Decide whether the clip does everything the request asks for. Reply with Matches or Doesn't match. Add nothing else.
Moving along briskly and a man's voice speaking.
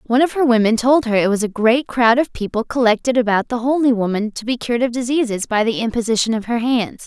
Doesn't match